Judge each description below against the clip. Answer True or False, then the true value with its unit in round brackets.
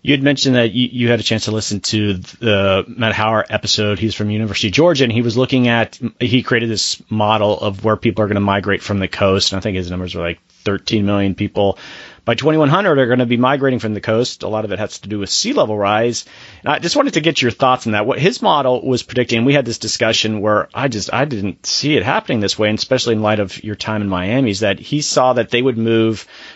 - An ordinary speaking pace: False (260 wpm)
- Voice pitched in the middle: False (110 Hz)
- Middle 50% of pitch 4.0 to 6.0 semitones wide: False (3.4 semitones)